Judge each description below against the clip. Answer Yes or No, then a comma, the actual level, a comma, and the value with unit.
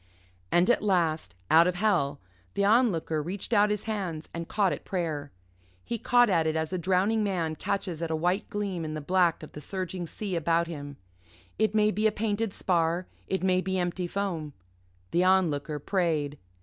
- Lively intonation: No, average, 3.8 semitones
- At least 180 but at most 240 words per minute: Yes, average, 190 wpm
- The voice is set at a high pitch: No, medium, 180 Hz